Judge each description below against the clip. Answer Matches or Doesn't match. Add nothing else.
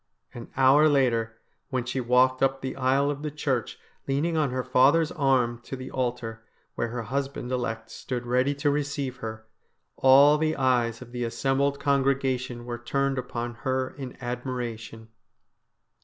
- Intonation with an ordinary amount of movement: Doesn't match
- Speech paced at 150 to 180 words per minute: Matches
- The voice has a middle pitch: Doesn't match